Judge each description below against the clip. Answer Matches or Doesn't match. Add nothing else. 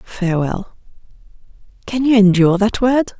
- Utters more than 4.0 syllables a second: Matches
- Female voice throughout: Matches